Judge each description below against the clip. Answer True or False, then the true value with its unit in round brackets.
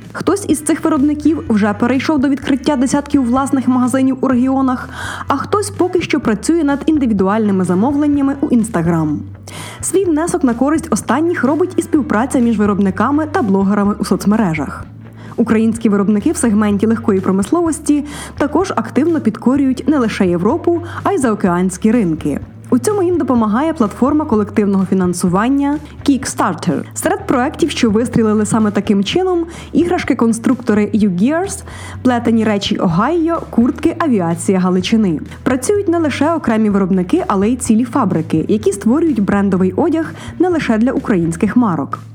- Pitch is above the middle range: True (240 Hz)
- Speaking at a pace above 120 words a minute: True (135 wpm)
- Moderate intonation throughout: False (6.4 semitones)